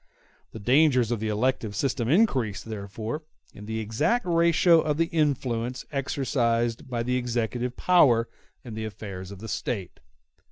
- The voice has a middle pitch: No, low, 120 Hz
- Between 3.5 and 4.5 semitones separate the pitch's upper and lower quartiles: Yes, average, 4.1 semitones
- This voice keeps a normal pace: Yes, average, 145 wpm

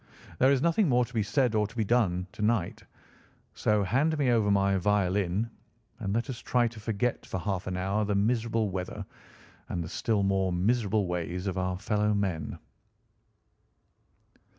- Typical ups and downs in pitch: Yes, average, 3.7 semitones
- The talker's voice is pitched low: Yes, low, 105 Hz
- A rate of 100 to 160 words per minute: No, average, 175 wpm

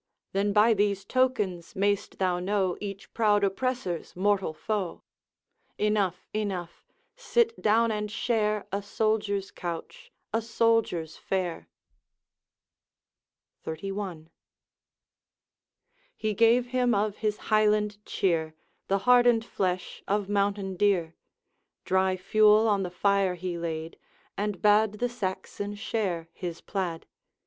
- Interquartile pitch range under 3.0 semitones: Yes, narrow, 2.6 semitones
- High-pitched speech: Yes, high, 205 Hz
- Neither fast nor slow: No, slow, 115 wpm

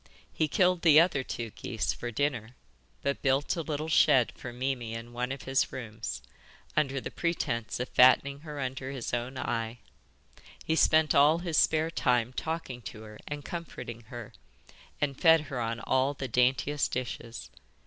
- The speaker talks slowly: No, average, 170 wpm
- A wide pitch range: No, average, 3.8 semitones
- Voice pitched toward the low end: Yes, low, 130 Hz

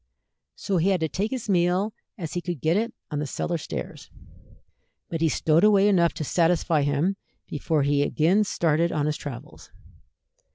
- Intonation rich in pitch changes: No, average, 4.0 semitones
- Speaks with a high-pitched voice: No, medium, 170 Hz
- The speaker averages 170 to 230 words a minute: Yes, average, 175 wpm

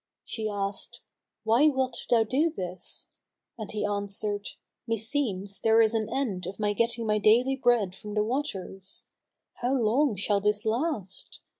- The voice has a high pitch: Yes, high, 220 Hz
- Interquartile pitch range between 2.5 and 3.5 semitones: Yes, average, 3.1 semitones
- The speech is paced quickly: No, average, 150 wpm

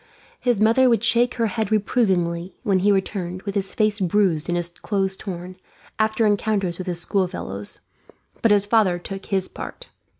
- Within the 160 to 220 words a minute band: Yes, average, 170 wpm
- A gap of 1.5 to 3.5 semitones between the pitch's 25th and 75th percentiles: Yes, average, 3.2 semitones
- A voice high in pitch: Yes, high, 195 Hz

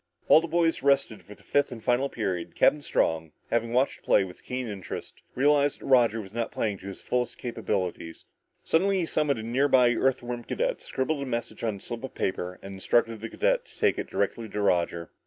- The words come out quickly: Yes, fast, 220 wpm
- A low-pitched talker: Yes, low, 120 Hz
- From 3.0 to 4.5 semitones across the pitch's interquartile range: No, average, 5.3 semitones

